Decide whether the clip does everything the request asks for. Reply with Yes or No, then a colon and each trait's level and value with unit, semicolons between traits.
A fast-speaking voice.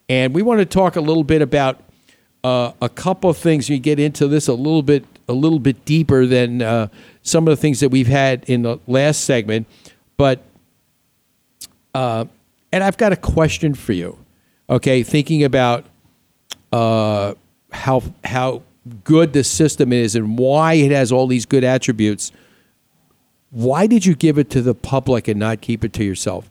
No: average, 180 wpm